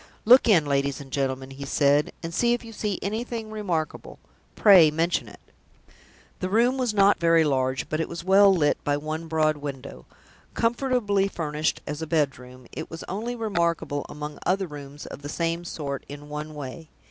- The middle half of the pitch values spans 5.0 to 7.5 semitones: Yes, wide, 5.5 semitones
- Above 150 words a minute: Yes, average, 175 wpm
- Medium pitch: Yes, medium, 160 Hz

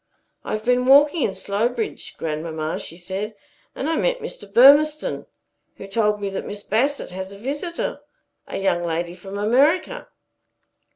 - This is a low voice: No, high, 210 Hz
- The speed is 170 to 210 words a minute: No, average, 155 wpm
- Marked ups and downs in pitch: Yes, wide, 6.5 semitones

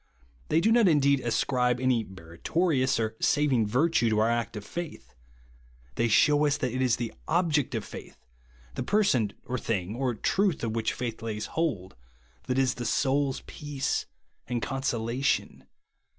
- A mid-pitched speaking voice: No, low, 125 Hz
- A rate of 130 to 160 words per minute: No, average, 170 wpm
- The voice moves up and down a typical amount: Yes, average, 4.4 semitones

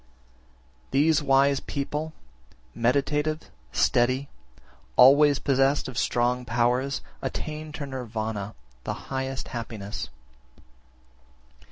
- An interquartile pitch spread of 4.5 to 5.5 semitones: No, average, 3.0 semitones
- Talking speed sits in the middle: No, slow, 85 wpm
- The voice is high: No, low, 135 Hz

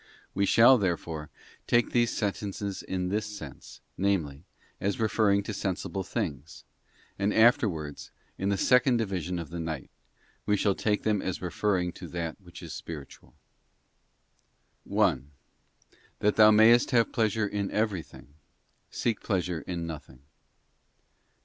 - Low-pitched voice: Yes, low, 100 Hz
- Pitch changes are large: No, average, 3.9 semitones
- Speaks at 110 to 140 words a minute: Yes, slow, 135 wpm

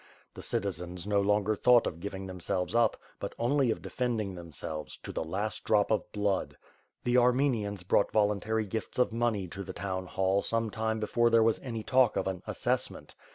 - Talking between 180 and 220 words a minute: Yes, average, 190 wpm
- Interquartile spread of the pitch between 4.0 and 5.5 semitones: No, average, 3.3 semitones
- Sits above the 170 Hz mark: No, low, 105 Hz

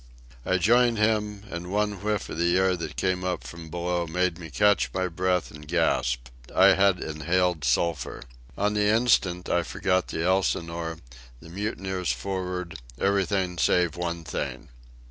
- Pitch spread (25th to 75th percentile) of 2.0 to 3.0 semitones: Yes, narrow, 2.6 semitones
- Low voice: Yes, very low, 90 Hz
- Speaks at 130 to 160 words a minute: Yes, average, 155 wpm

